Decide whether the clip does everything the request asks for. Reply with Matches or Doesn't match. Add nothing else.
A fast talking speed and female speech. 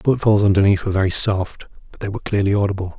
Doesn't match